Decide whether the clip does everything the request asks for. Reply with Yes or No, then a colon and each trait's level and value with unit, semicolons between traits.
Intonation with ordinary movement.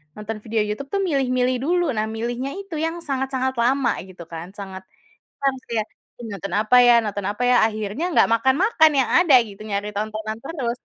Yes: average, 4.5 semitones